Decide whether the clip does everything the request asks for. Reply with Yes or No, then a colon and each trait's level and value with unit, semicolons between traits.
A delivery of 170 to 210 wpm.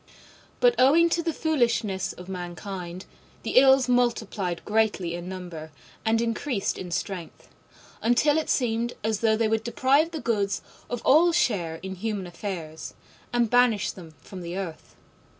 No: average, 150 wpm